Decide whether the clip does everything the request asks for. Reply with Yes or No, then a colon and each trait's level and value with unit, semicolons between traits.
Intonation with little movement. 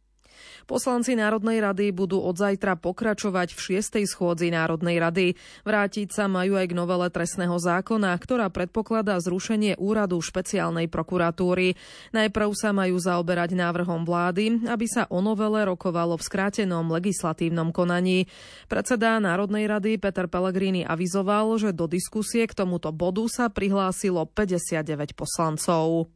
No: average, 3.2 semitones